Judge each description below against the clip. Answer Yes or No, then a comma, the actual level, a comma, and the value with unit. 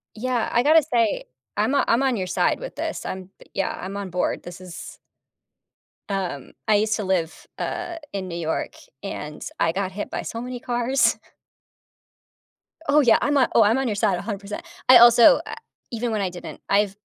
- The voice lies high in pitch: Yes, high, 215 Hz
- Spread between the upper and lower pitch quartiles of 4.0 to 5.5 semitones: Yes, average, 4.4 semitones